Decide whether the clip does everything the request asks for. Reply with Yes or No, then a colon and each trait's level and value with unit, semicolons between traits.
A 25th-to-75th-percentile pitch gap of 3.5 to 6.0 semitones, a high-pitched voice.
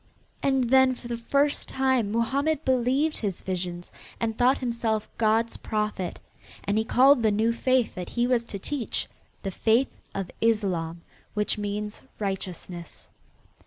Yes: average, 4.0 semitones; high, 230 Hz